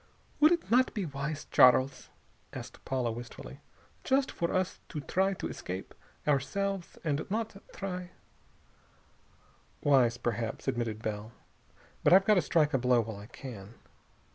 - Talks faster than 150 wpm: No, average, 145 wpm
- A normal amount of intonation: No, wide, 8.1 semitones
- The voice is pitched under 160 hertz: Yes, medium, 140 Hz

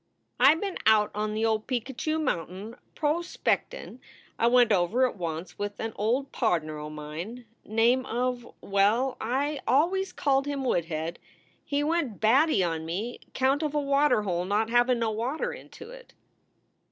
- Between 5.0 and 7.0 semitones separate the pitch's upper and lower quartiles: Yes, average, 5.3 semitones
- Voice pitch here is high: Yes, high, 235 Hz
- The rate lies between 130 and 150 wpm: No, average, 165 wpm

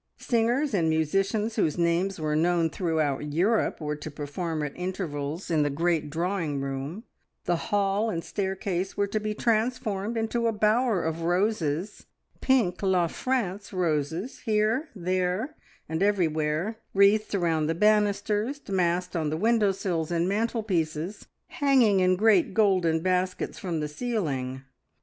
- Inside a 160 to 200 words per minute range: No, average, 140 wpm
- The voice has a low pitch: No, medium, 185 Hz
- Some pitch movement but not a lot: Yes, average, 4.8 semitones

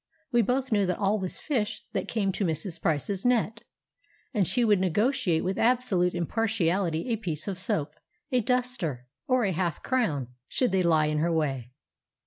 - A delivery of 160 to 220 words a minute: Yes, average, 175 wpm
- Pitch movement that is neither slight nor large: No, wide, 5.8 semitones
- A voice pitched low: No, high, 195 Hz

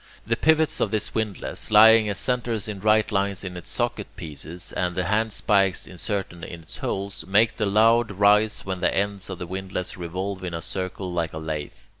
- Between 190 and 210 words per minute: Yes, average, 195 wpm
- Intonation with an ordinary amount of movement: Yes, average, 3.1 semitones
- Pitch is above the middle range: No, low, 100 Hz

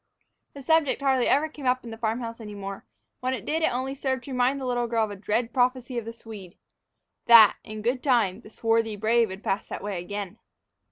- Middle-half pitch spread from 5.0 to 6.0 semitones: No, average, 3.2 semitones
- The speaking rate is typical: No, fast, 230 wpm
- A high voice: Yes, high, 235 Hz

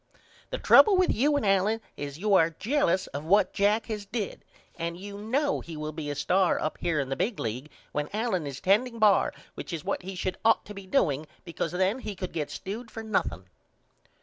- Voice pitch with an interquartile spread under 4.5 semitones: No, average, 5.2 semitones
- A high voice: Yes, high, 195 Hz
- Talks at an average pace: No, fast, 215 wpm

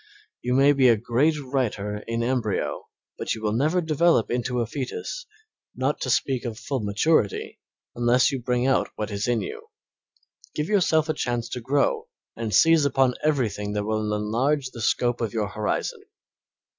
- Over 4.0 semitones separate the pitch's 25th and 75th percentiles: Yes, average, 4.4 semitones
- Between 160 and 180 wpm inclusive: Yes, average, 170 wpm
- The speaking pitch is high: No, low, 125 Hz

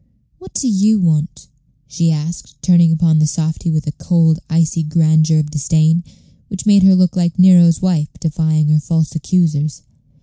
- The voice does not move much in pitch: Yes, narrow, 2.1 semitones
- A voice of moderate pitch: Yes, medium, 160 Hz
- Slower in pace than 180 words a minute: Yes, average, 165 wpm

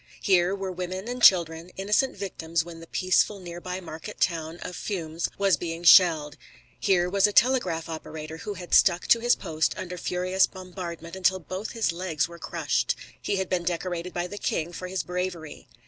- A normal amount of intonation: No, narrow, 2.1 semitones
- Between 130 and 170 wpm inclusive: No, average, 180 wpm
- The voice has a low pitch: No, medium, 180 Hz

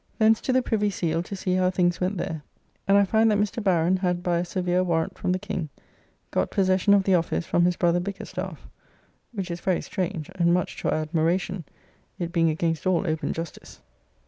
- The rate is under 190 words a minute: No, fast, 205 wpm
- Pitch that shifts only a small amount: Yes, narrow, 2.2 semitones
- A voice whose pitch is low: No, medium, 180 Hz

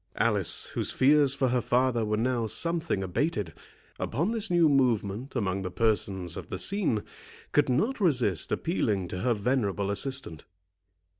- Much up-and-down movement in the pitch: Yes, wide, 6.3 semitones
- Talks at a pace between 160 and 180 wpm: No, average, 150 wpm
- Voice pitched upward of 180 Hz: No, low, 125 Hz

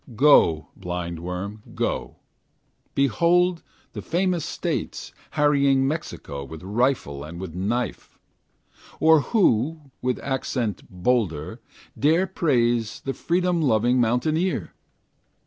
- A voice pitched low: Yes, low, 125 Hz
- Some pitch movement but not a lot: No, wide, 8.4 semitones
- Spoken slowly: Yes, slow, 95 wpm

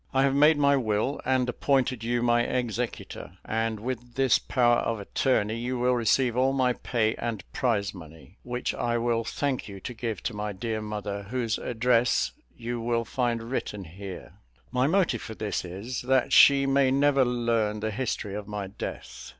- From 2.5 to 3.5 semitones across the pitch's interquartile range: Yes, average, 3.1 semitones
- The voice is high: No, low, 120 Hz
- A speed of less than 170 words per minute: No, average, 180 wpm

